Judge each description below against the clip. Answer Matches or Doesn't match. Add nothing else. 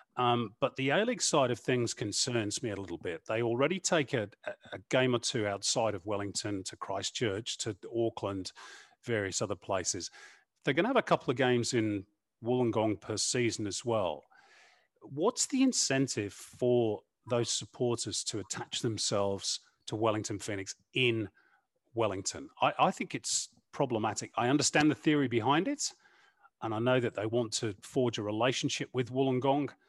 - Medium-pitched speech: Doesn't match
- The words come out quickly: Doesn't match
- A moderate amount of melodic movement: Matches